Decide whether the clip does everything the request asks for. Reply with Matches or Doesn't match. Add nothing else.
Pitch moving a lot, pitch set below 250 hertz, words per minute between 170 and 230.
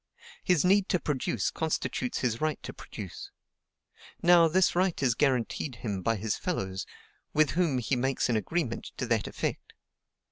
Doesn't match